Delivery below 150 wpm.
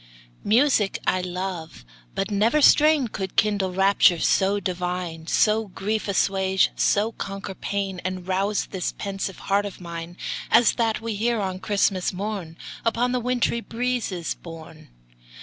Yes: average, 140 wpm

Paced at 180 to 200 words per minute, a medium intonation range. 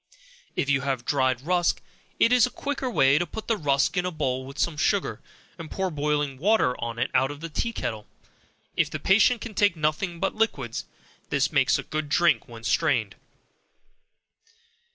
No: average, 185 wpm; wide, 6.1 semitones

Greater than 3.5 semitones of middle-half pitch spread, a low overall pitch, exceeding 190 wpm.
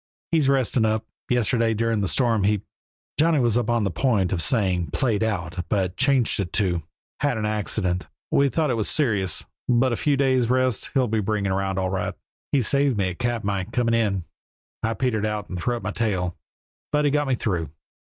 Yes: average, 4.5 semitones; low, 110 Hz; average, 200 wpm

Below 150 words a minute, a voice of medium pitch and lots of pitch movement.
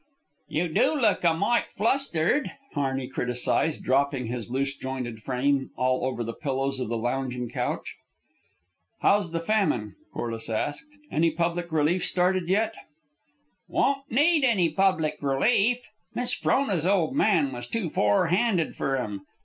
Yes: average, 140 wpm; medium, 155 Hz; wide, 7.2 semitones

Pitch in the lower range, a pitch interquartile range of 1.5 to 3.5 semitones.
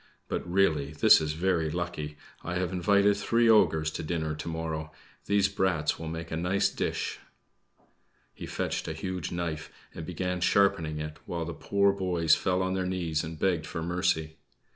Yes: very low, 85 Hz; average, 2.9 semitones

